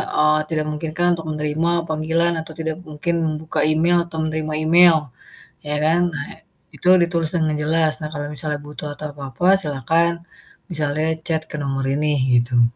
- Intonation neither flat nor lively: No, narrow, 1.7 semitones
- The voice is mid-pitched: Yes, medium, 155 Hz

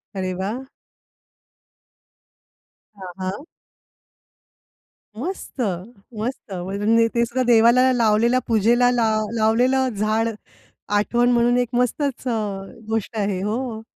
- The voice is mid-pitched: No, high, 230 Hz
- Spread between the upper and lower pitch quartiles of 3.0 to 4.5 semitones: No, narrow, 2.6 semitones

